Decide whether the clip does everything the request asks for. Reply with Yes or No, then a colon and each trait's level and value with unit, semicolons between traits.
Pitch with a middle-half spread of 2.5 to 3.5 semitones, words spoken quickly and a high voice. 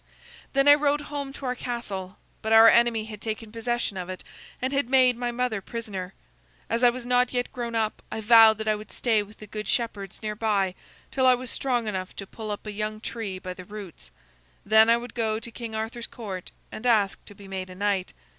Yes: average, 2.8 semitones; fast, 225 wpm; high, 220 Hz